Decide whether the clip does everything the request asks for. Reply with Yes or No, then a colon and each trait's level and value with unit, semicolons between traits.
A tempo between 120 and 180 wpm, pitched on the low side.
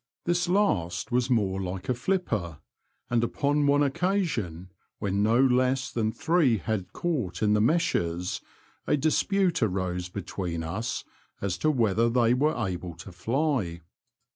Yes: average, 140 wpm; low, 115 Hz